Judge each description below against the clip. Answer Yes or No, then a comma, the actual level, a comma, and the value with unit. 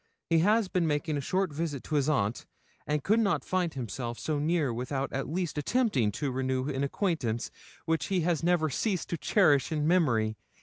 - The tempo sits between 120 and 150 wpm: No, average, 190 wpm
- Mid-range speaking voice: Yes, medium, 150 Hz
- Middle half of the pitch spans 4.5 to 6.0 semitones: Yes, average, 4.8 semitones